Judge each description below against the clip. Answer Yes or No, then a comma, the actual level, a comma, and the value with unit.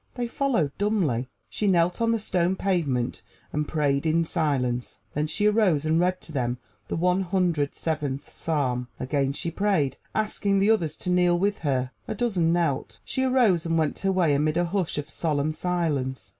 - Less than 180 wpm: No, average, 185 wpm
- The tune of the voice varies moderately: Yes, average, 4.9 semitones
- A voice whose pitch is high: No, medium, 165 Hz